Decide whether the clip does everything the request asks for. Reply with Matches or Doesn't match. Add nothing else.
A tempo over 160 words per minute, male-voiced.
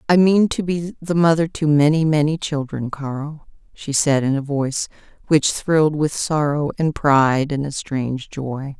Doesn't match